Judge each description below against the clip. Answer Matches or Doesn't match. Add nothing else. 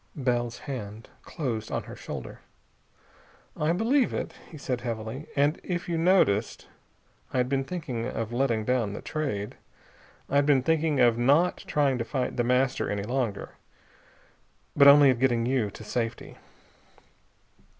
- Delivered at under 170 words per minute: Matches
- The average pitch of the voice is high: Doesn't match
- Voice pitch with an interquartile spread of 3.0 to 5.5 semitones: Matches